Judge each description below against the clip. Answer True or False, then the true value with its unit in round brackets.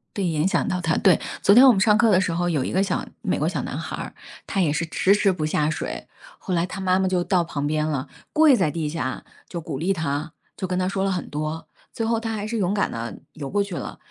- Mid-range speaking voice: True (180 Hz)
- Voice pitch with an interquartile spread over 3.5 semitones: True (4.0 semitones)